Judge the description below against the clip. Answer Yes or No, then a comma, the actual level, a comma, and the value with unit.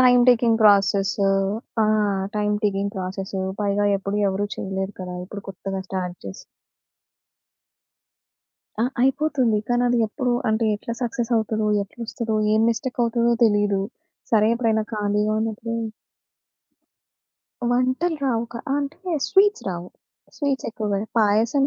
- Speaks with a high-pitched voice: Yes, high, 220 Hz